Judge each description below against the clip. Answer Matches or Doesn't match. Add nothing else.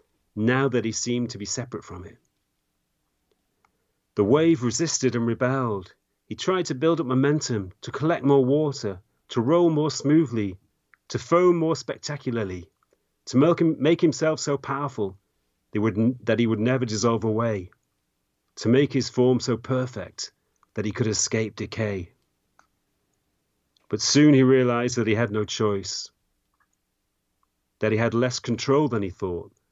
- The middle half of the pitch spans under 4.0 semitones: Doesn't match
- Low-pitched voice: Matches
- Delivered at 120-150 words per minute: Matches